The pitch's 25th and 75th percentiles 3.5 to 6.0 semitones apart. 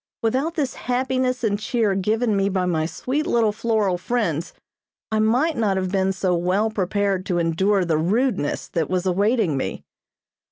Yes: average, 4.4 semitones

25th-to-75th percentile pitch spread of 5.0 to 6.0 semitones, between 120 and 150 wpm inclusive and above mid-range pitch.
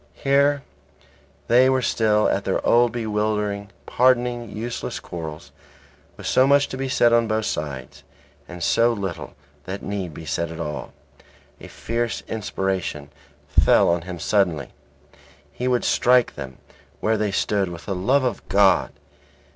No: wide, 5.4 semitones; average, 145 wpm; low, 105 Hz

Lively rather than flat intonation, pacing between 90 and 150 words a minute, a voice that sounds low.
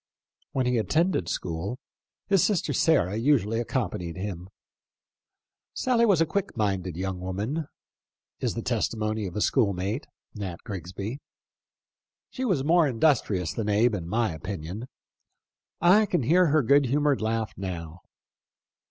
Yes: wide, 7.9 semitones; slow, 135 wpm; low, 110 Hz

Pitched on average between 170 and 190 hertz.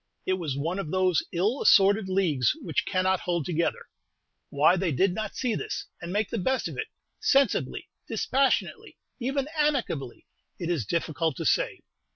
Yes: medium, 185 Hz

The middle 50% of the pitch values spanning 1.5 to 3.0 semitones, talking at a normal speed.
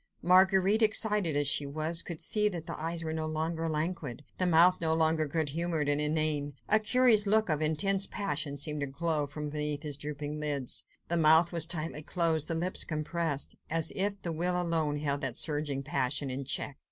Yes: average, 2.7 semitones; average, 195 wpm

